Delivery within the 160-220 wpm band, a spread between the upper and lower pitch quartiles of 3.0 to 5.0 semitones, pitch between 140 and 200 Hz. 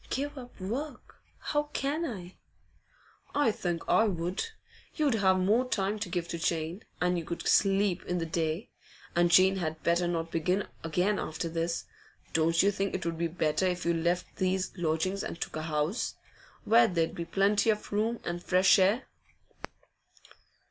Yes: average, 170 wpm; average, 3.7 semitones; medium, 185 Hz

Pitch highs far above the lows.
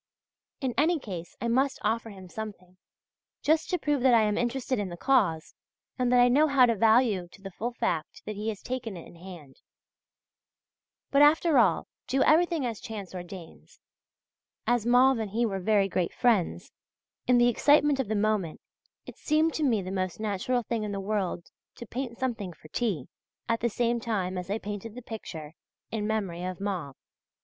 No: average, 4.6 semitones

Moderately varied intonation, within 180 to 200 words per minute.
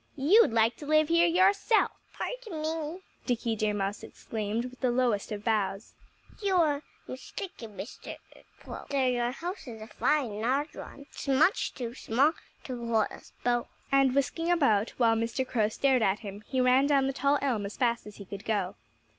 Yes: average, 4.9 semitones; average, 185 wpm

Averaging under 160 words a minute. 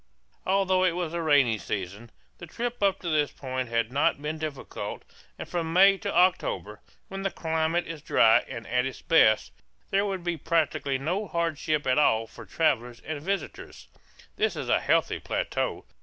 No: average, 175 wpm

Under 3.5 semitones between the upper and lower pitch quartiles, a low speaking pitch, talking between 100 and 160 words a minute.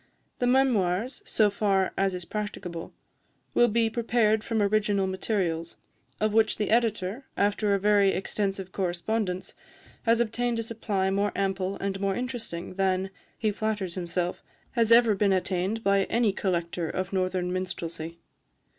No: average, 2.8 semitones; high, 200 Hz; average, 145 wpm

